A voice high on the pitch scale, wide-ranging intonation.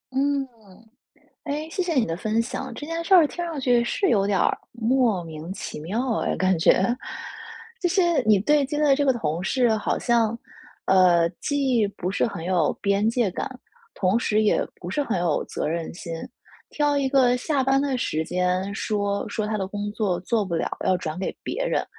Yes: high, 220 Hz; wide, 6.6 semitones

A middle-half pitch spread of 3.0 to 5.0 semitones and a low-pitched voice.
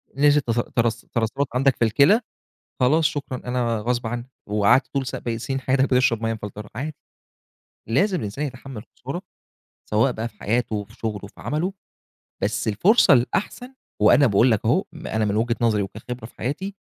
Yes: average, 4.0 semitones; low, 120 Hz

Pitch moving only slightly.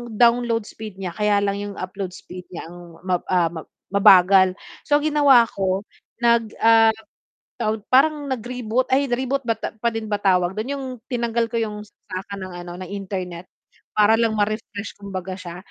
No: average, 3.8 semitones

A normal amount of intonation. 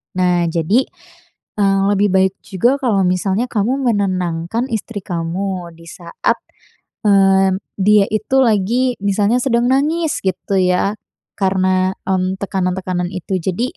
Yes: average, 3.3 semitones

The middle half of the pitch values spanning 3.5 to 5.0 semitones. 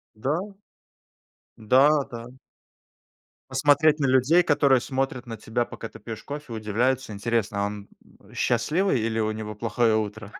Yes: average, 4.0 semitones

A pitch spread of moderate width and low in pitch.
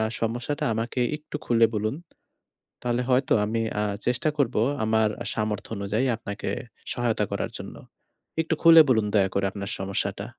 Yes: average, 3.1 semitones; low, 115 Hz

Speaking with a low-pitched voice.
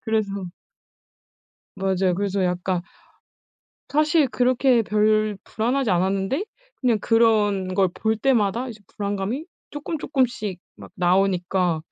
No: high, 210 Hz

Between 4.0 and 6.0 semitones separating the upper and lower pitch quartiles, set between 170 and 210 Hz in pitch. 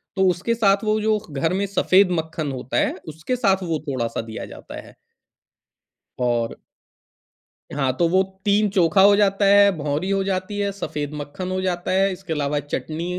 Yes: average, 5.0 semitones; medium, 185 Hz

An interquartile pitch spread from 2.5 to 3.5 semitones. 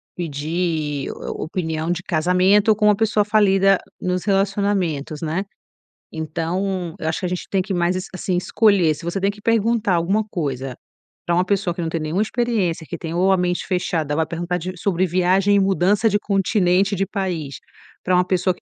Yes: average, 2.9 semitones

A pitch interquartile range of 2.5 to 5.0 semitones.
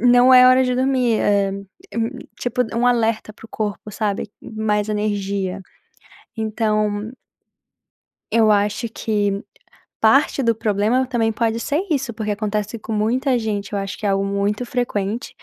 Yes: average, 2.8 semitones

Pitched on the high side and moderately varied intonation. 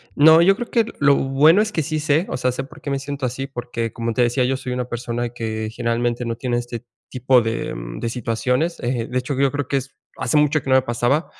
No: low, 130 Hz; average, 3.0 semitones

